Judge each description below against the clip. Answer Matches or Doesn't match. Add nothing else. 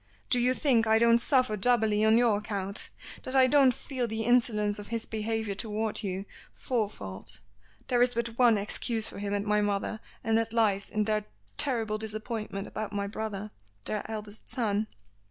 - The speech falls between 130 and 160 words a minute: Doesn't match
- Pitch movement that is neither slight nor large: Doesn't match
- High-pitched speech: Matches